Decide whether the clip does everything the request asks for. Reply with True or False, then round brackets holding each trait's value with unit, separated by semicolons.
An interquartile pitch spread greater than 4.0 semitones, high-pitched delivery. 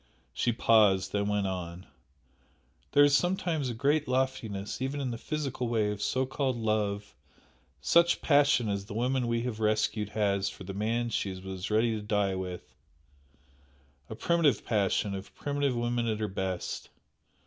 False (4.4 semitones; 110 Hz)